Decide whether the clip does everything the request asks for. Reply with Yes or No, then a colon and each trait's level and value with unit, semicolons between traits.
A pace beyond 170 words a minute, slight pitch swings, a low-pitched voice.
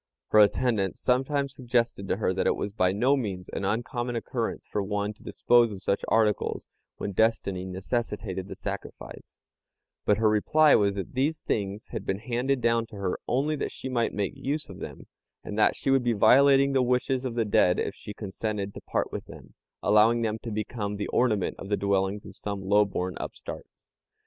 No: average, 195 wpm; average, 3.6 semitones; low, 110 Hz